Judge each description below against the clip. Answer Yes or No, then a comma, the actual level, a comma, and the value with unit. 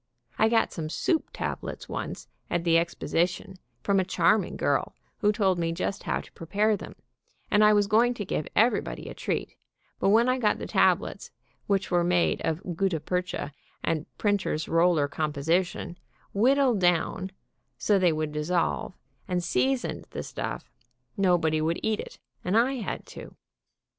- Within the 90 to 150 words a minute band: No, average, 160 wpm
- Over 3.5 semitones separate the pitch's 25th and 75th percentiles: Yes, average, 3.9 semitones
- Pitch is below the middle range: No, medium, 180 Hz